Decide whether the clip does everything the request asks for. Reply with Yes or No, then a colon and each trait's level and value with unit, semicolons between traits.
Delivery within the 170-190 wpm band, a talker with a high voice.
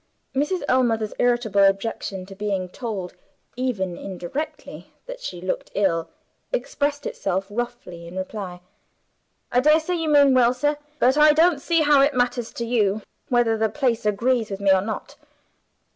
No: average, 155 wpm; high, 235 Hz